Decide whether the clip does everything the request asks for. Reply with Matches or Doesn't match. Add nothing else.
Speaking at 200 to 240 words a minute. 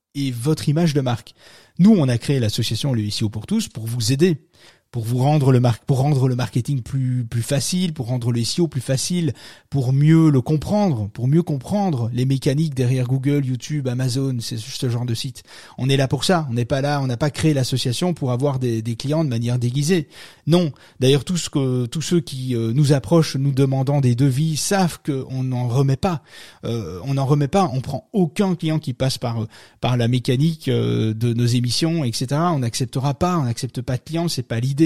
Matches